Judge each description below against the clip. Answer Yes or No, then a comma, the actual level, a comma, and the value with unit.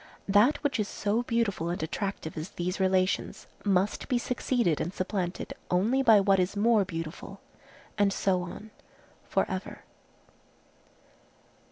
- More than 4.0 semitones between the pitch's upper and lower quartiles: No, average, 3.3 semitones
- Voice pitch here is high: Yes, high, 195 Hz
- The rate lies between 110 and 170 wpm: Yes, slow, 135 wpm